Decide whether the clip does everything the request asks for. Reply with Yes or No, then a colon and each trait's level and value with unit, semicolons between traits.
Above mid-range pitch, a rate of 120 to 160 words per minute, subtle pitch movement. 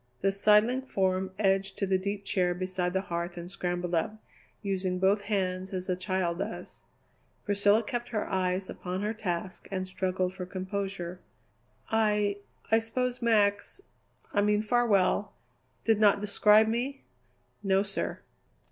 Yes: high, 195 Hz; average, 145 wpm; narrow, 2.2 semitones